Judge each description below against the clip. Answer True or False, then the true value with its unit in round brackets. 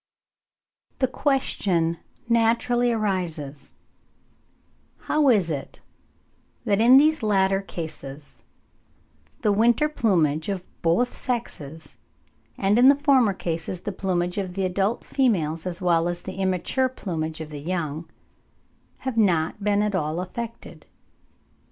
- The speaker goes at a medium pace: False (120 wpm)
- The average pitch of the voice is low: False (190 Hz)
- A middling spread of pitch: False (5.9 semitones)